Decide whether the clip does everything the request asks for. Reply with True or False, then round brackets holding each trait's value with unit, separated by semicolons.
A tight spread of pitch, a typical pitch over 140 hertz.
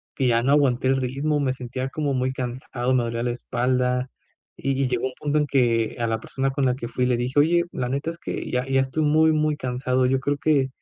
False (2.2 semitones; 130 Hz)